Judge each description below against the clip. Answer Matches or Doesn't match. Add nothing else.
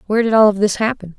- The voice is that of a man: Doesn't match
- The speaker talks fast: Matches